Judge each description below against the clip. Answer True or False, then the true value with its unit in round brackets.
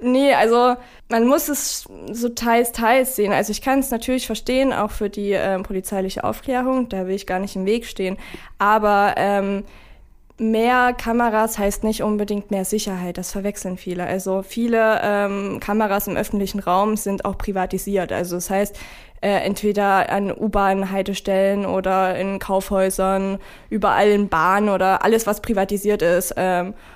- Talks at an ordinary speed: True (160 wpm)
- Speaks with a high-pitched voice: True (200 Hz)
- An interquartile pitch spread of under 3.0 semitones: True (2.5 semitones)